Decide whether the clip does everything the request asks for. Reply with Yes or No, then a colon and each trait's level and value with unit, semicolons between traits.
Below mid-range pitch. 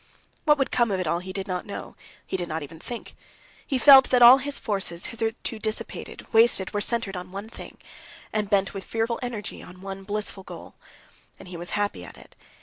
No: high, 205 Hz